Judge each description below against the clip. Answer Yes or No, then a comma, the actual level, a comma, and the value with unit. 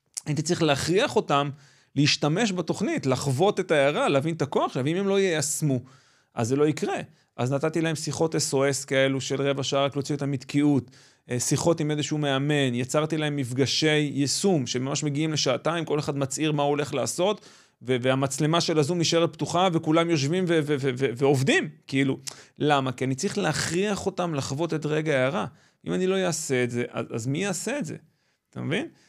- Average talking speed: No, fast, 180 wpm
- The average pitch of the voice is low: No, medium, 145 Hz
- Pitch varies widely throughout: No, average, 3.1 semitones